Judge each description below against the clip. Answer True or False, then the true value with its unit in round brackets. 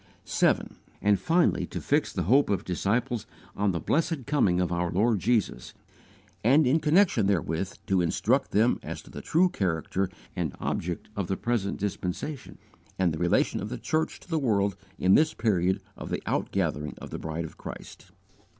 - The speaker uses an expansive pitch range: True (6.9 semitones)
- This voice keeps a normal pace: True (180 wpm)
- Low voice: True (100 Hz)